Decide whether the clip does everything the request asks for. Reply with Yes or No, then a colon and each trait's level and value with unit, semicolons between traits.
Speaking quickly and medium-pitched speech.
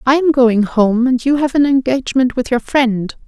No: fast, 220 wpm; very high, 255 Hz